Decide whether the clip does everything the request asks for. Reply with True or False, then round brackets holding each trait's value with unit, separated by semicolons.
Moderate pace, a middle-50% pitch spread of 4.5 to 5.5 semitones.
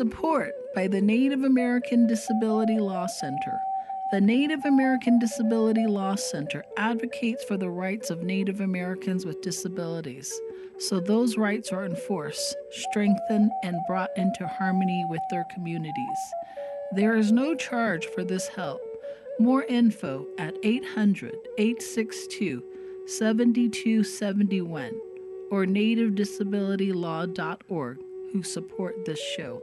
False (110 wpm; 5.1 semitones)